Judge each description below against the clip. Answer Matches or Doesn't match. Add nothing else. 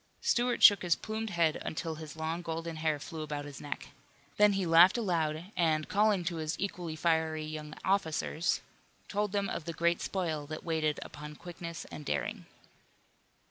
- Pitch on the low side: Doesn't match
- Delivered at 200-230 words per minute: Doesn't match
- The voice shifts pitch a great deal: Doesn't match